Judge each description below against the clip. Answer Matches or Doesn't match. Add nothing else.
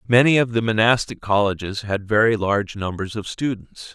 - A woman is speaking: Doesn't match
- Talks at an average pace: Matches